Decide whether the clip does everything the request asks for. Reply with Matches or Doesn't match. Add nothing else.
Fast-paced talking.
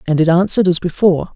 Matches